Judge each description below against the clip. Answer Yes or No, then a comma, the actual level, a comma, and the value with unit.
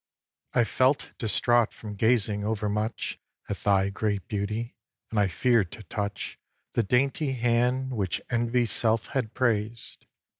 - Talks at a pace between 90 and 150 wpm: Yes, average, 145 wpm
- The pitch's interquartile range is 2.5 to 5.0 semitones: Yes, average, 2.8 semitones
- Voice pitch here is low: Yes, low, 110 Hz